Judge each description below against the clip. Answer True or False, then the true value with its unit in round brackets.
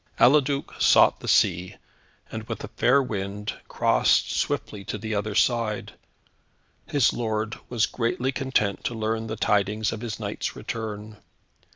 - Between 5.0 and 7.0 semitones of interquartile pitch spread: False (2.4 semitones)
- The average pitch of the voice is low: True (110 Hz)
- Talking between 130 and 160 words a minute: True (145 wpm)